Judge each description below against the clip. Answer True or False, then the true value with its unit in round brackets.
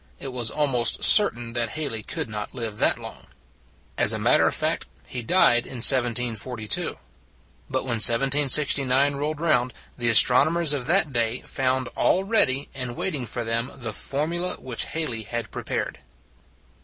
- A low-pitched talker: True (130 Hz)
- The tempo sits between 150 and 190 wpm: True (160 wpm)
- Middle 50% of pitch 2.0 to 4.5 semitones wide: True (3.6 semitones)